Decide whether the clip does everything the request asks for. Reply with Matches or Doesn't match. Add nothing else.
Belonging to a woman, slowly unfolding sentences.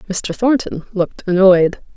Matches